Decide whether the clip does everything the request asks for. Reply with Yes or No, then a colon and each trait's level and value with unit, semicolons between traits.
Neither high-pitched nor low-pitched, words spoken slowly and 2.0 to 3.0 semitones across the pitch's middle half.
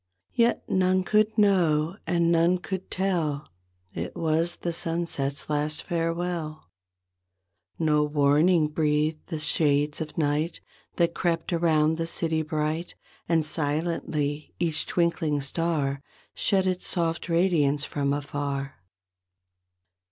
Yes: medium, 160 Hz; slow, 115 wpm; narrow, 2.4 semitones